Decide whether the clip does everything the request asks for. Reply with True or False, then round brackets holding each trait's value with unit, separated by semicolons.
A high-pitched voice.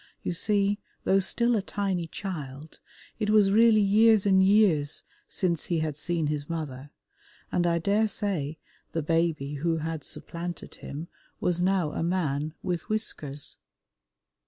False (175 Hz)